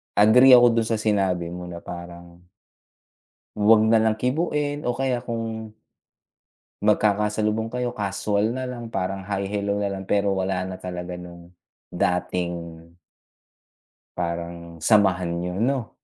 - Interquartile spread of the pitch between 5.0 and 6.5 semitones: No, average, 4.1 semitones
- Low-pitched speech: Yes, low, 100 Hz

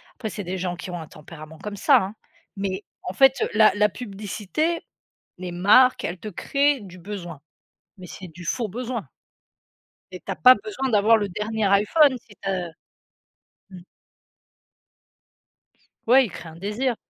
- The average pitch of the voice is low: No, high, 205 Hz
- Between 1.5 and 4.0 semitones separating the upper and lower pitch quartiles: No, average, 4.7 semitones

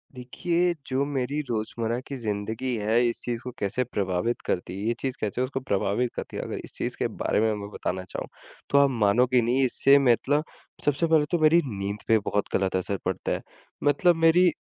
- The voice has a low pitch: Yes, low, 120 Hz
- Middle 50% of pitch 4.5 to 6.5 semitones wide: Yes, average, 5.1 semitones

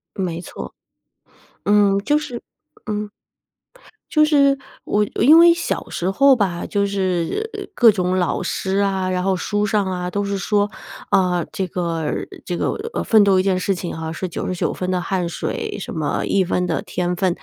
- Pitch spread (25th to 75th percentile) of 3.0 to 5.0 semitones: No, narrow, 2.6 semitones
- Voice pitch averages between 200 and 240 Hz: No, high, 190 Hz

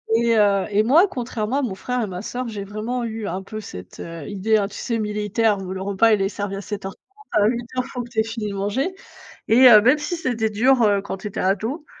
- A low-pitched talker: No, high, 215 Hz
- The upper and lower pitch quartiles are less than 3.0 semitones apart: No, average, 3.4 semitones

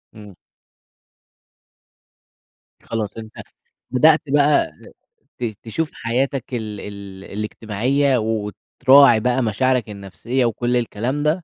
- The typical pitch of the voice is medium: No, low, 120 Hz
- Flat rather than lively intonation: No, average, 3.9 semitones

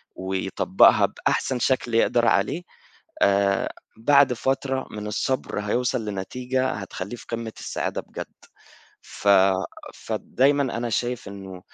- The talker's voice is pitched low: Yes, low, 115 Hz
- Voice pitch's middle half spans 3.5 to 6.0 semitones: Yes, average, 4.5 semitones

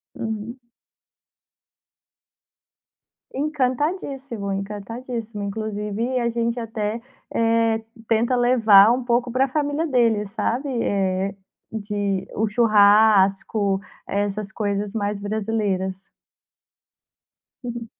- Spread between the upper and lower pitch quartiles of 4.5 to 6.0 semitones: No, average, 2.9 semitones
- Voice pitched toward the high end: Yes, high, 220 Hz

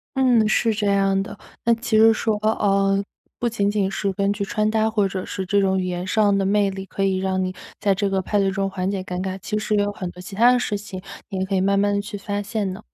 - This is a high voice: Yes, high, 200 Hz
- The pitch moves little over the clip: Yes, narrow, 1.8 semitones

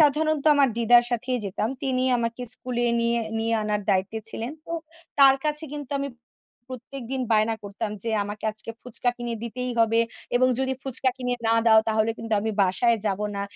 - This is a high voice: Yes, high, 235 Hz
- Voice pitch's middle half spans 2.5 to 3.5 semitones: Yes, average, 2.8 semitones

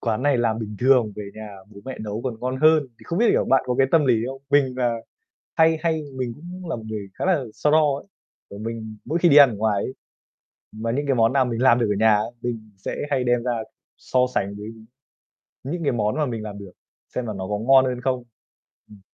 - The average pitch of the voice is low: Yes, low, 125 Hz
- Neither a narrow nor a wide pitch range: Yes, average, 4.0 semitones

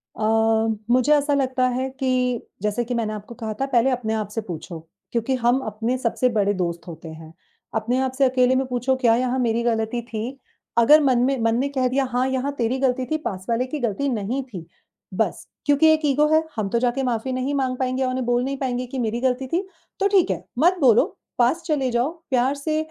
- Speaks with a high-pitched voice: Yes, very high, 250 Hz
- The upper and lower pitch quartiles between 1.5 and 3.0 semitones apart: Yes, average, 2.7 semitones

